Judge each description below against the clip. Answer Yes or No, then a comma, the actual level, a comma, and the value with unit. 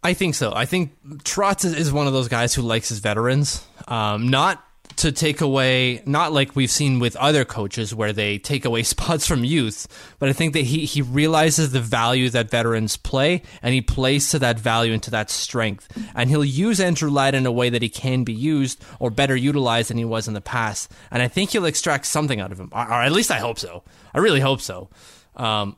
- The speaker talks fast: Yes, fast, 230 wpm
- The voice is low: Yes, low, 130 Hz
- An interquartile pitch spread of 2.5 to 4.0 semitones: No, average, 4.4 semitones